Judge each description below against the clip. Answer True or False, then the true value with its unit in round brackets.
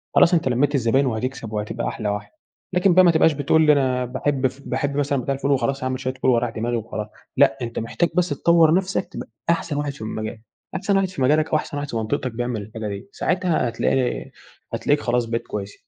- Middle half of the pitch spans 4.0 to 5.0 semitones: True (4.6 semitones)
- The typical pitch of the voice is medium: False (130 Hz)